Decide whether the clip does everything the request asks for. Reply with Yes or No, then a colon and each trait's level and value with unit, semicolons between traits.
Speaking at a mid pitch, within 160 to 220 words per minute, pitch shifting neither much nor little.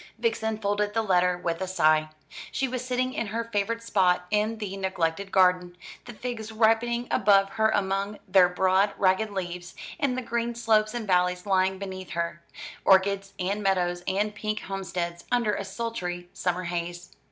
No: high, 195 Hz; average, 165 wpm; average, 3.4 semitones